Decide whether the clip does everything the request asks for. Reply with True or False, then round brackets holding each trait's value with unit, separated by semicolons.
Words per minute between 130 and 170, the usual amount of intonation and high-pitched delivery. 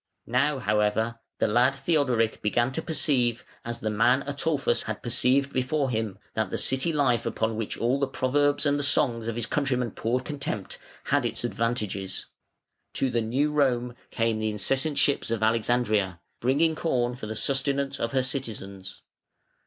False (165 wpm; 3.8 semitones; 125 Hz)